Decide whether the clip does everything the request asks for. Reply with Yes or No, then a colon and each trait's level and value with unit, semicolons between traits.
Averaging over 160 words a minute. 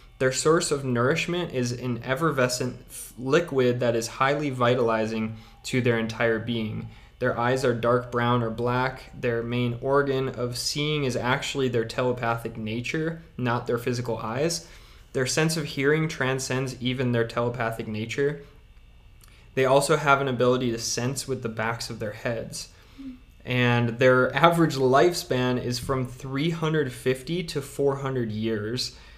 No: average, 140 wpm